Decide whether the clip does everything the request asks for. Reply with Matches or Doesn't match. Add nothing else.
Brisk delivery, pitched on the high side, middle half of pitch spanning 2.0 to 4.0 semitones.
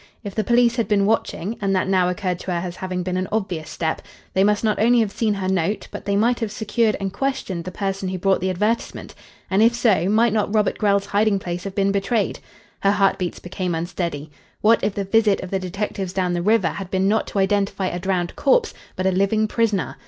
Matches